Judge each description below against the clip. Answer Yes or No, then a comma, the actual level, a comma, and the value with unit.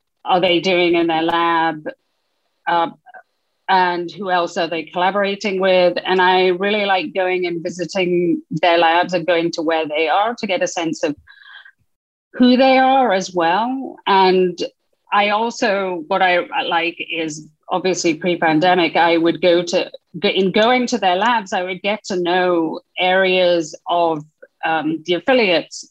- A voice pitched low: No, medium, 180 Hz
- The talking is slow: No, average, 155 wpm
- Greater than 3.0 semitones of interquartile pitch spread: No, average, 2.7 semitones